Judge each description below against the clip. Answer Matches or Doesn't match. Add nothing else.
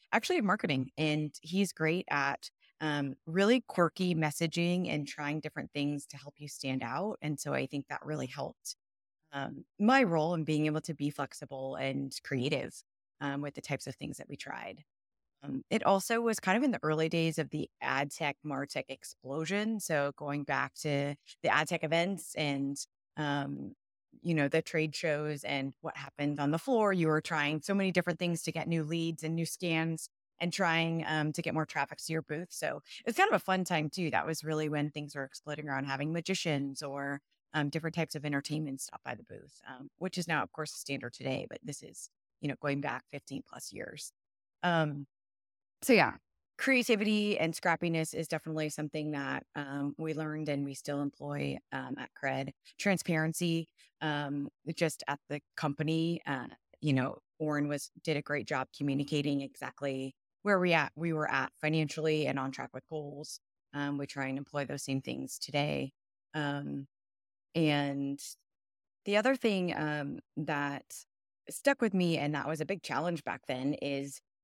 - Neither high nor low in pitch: Matches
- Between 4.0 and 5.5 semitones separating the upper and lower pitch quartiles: Doesn't match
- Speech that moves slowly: Doesn't match